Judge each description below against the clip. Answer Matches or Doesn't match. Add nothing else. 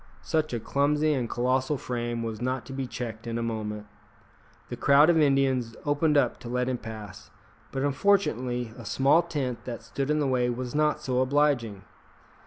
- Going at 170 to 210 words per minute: Matches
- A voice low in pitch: Matches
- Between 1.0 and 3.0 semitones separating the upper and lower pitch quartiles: Doesn't match